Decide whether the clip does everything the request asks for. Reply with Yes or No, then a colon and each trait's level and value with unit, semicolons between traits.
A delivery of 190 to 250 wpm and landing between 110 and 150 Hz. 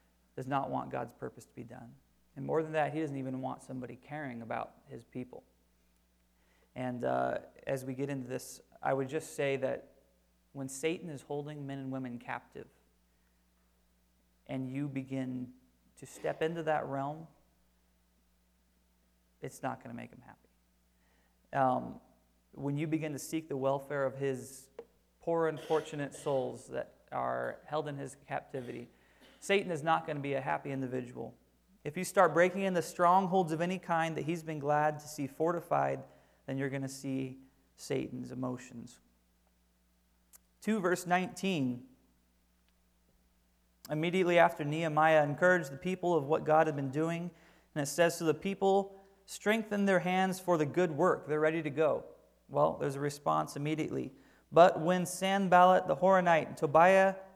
No: average, 160 wpm; medium, 140 Hz